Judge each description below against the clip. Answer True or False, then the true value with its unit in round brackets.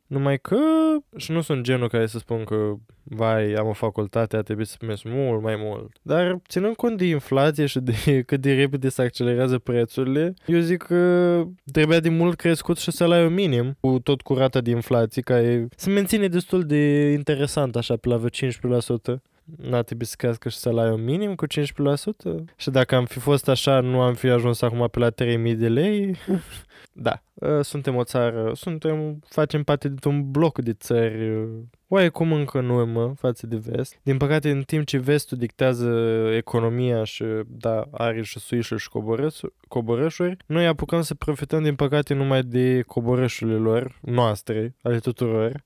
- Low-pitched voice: True (130 Hz)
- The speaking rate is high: True (175 wpm)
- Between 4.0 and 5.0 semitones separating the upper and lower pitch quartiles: True (4.5 semitones)